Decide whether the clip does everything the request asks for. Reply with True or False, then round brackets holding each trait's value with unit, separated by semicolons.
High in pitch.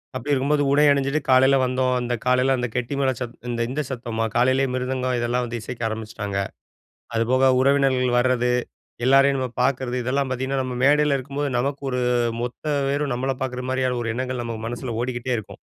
False (130 Hz)